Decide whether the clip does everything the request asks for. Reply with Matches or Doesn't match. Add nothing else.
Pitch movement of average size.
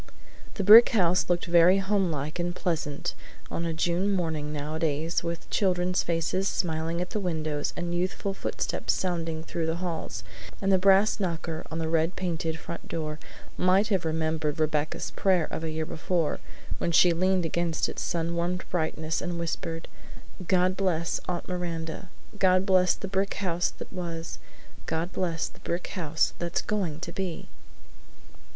Doesn't match